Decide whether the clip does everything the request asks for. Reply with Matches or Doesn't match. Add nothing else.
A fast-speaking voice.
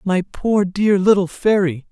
Doesn't match